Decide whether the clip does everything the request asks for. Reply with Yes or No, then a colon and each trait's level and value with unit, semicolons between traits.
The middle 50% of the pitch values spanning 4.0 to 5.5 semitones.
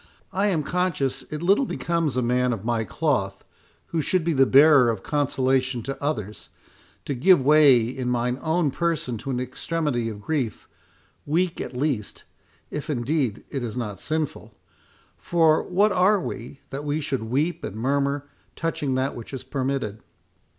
Yes: average, 4.3 semitones